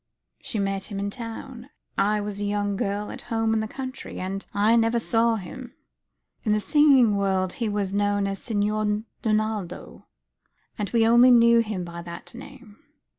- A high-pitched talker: Yes, high, 210 Hz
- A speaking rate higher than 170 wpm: Yes, average, 180 wpm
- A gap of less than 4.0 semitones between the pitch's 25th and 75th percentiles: Yes, narrow, 2.5 semitones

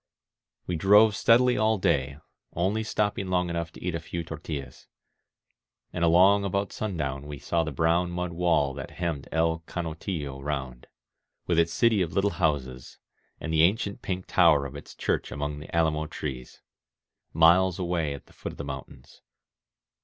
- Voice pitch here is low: Yes, very low, 85 Hz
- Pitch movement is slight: No, average, 4.0 semitones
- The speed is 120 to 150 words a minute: No, average, 170 wpm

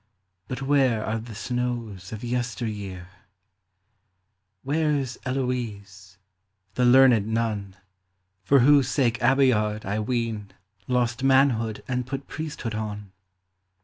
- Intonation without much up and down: No, average, 3.4 semitones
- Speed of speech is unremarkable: No, slow, 115 wpm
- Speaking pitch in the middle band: No, low, 120 Hz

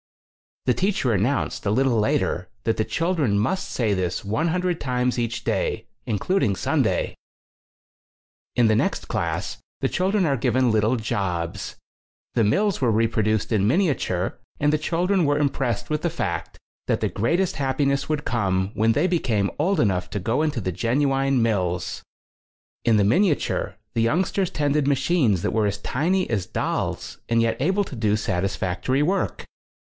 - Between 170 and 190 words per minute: No, average, 160 wpm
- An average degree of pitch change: No, wide, 6.4 semitones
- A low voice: Yes, low, 125 Hz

